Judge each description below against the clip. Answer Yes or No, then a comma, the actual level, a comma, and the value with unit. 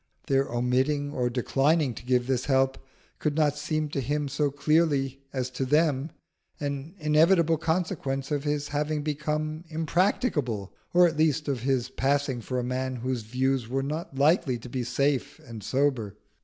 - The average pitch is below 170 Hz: Yes, medium, 140 Hz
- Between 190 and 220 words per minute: No, average, 165 wpm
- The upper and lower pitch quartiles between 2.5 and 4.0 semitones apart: Yes, average, 2.9 semitones